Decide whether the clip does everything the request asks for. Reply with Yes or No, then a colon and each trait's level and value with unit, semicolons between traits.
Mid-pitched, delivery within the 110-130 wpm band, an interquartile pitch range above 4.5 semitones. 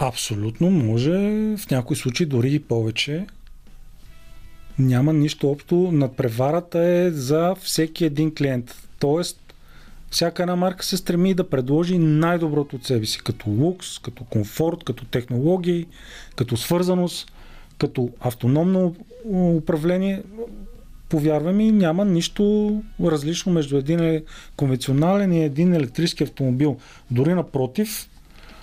Yes: medium, 160 Hz; slow, 115 wpm; average, 5.1 semitones